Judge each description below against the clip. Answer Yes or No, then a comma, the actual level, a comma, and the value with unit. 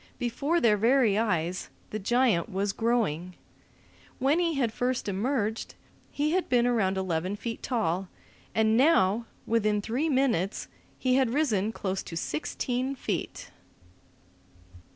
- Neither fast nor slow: No, slow, 130 wpm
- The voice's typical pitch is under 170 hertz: No, high, 225 Hz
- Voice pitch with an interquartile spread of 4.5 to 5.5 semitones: Yes, average, 4.8 semitones